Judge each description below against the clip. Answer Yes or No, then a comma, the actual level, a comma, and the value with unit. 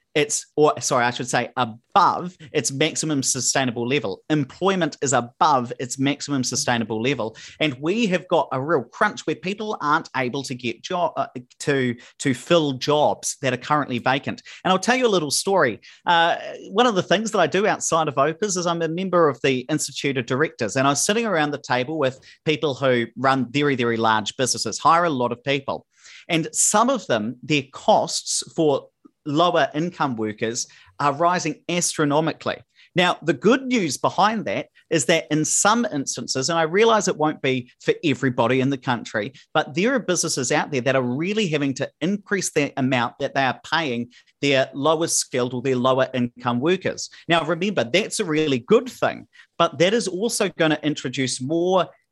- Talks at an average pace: Yes, average, 190 wpm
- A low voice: No, medium, 150 Hz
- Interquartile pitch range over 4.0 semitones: Yes, average, 4.8 semitones